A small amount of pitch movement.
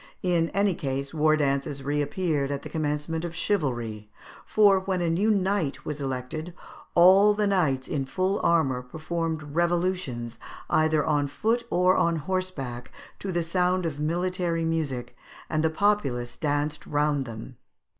No: average, 4.6 semitones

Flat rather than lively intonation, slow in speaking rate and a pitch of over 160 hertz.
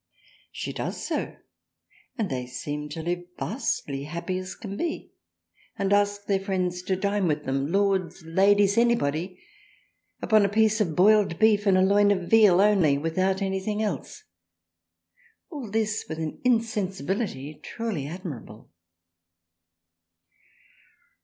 No: average, 4.1 semitones; slow, 130 wpm; high, 190 Hz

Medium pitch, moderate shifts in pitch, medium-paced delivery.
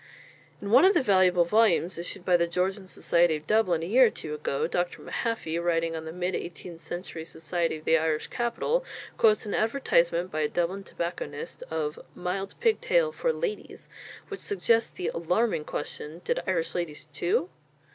Yes: medium, 175 Hz; average, 4.6 semitones; average, 175 wpm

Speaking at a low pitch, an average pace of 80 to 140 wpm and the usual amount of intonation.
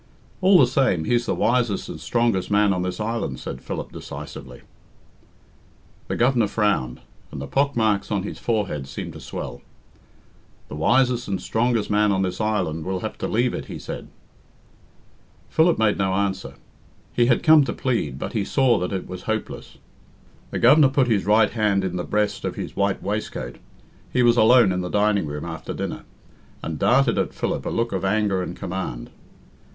No: low, 105 Hz; average, 180 wpm; average, 4.4 semitones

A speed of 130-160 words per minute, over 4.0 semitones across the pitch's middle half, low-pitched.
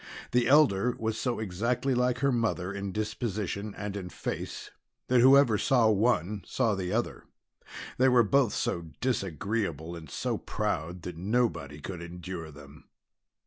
Yes: average, 145 wpm; average, 5.3 semitones; low, 105 Hz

